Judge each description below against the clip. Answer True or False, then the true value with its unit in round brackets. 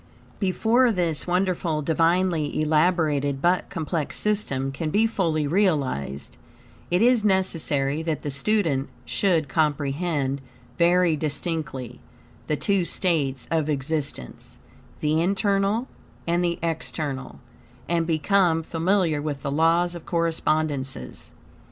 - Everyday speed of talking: False (110 wpm)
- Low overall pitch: False (160 Hz)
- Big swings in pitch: False (3.8 semitones)